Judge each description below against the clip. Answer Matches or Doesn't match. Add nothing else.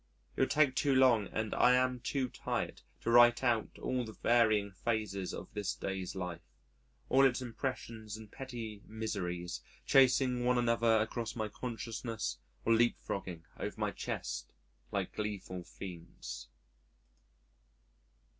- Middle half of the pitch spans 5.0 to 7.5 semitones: Doesn't match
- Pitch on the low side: Matches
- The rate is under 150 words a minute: Matches